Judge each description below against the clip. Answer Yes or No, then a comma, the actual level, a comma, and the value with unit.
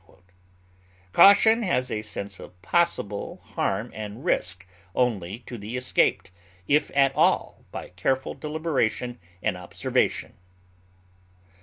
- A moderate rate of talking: No, slow, 110 wpm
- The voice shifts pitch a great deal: Yes, wide, 5.8 semitones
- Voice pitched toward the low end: Yes, low, 120 Hz